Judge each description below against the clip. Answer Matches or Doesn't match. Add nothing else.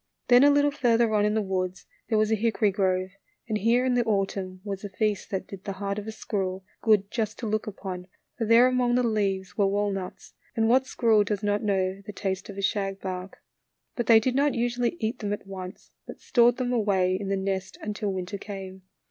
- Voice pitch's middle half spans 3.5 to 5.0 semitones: Doesn't match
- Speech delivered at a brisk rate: Matches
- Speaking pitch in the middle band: Doesn't match